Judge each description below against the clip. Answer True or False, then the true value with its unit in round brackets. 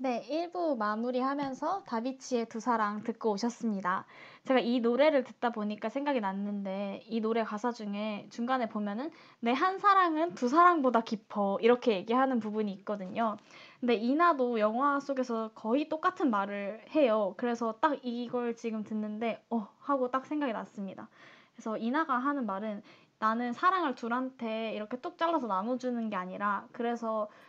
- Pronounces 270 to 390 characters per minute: True (340 characters per minute)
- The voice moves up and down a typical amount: True (3.8 semitones)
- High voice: True (235 Hz)